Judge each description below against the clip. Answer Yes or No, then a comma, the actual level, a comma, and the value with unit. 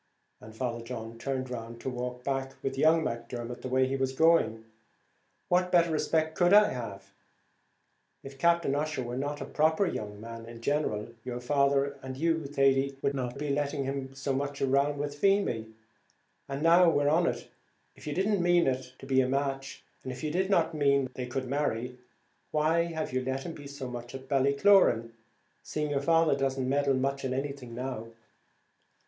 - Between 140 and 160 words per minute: No, average, 185 wpm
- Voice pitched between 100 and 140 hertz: Yes, low, 135 Hz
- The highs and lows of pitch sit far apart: No, average, 3.0 semitones